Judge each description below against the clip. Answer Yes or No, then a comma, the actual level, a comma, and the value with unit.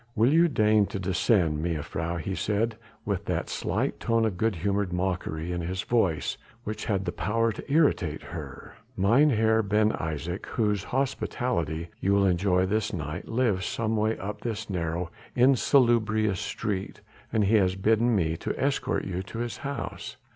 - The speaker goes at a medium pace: Yes, average, 160 wpm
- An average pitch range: Yes, average, 4.1 semitones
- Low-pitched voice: Yes, low, 100 Hz